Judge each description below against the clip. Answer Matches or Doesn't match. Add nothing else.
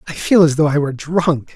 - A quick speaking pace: Matches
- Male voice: Matches